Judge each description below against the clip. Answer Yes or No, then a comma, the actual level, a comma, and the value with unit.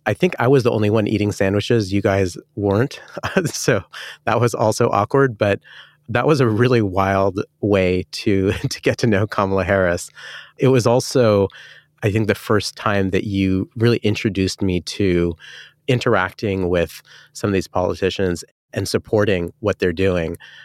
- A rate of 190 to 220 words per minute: No, average, 165 wpm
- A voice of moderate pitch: No, low, 105 Hz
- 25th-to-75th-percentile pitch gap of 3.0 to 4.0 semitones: Yes, average, 3.6 semitones